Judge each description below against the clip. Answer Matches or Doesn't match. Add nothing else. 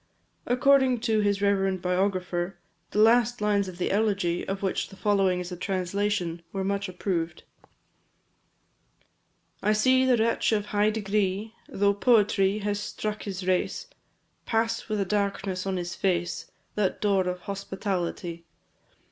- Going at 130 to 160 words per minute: Matches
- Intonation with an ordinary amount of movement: Doesn't match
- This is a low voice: Doesn't match